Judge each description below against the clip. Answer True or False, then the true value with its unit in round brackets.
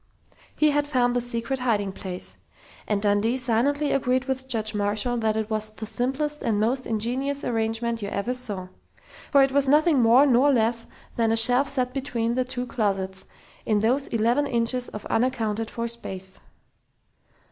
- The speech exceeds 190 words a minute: False (170 wpm)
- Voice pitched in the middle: False (235 Hz)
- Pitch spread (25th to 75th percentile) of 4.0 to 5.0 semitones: False (3.1 semitones)